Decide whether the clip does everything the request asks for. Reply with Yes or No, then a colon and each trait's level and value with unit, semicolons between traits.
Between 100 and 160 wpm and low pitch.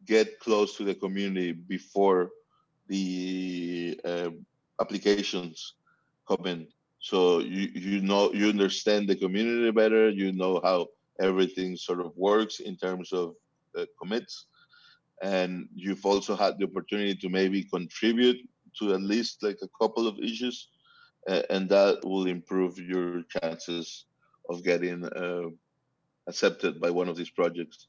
Yes: average, 140 wpm; very low, 95 Hz